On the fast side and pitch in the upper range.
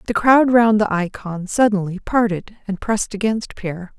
No: average, 165 wpm; high, 205 Hz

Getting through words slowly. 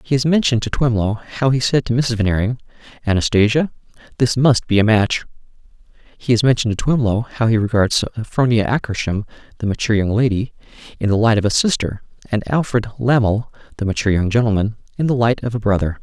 No: average, 185 wpm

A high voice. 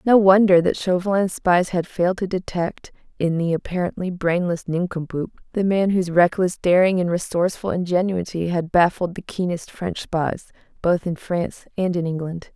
No: medium, 180 Hz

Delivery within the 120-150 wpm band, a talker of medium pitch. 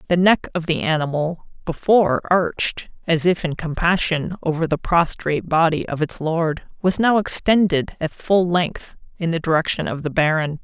No: average, 170 wpm; medium, 165 Hz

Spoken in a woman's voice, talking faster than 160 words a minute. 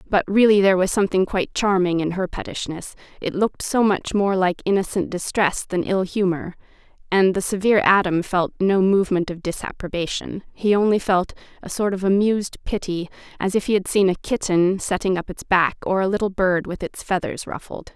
Yes: female; average, 190 wpm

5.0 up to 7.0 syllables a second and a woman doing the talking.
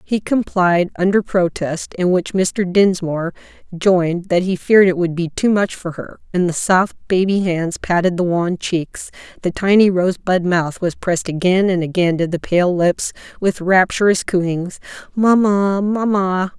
No: 4.4 syllables/s; female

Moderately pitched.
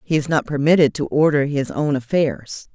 Yes: medium, 145 Hz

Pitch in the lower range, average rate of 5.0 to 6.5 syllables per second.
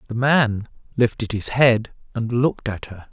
No: low, 115 Hz; 4.5 syllables/s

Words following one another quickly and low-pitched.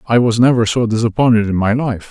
Yes: fast, 230 wpm; low, 115 Hz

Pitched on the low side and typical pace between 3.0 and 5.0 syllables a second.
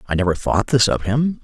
No: low, 120 Hz; 5.5 syllables/s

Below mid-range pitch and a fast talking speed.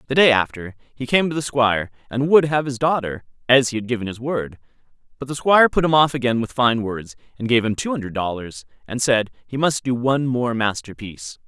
Yes: low, 125 Hz; fast, 225 wpm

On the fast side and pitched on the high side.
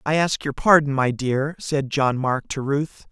No: fast, 210 wpm; medium, 140 Hz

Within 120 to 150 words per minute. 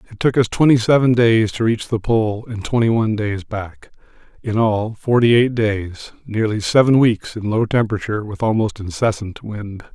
No: average, 170 wpm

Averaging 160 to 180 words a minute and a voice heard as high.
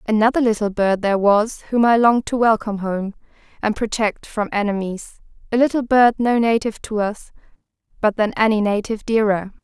Yes: average, 170 wpm; high, 215 Hz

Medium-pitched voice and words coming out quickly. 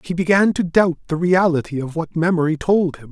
Yes: medium, 170 Hz; fast, 210 wpm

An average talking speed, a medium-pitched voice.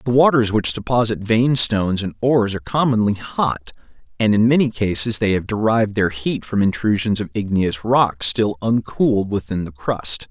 No: average, 175 wpm; low, 110 Hz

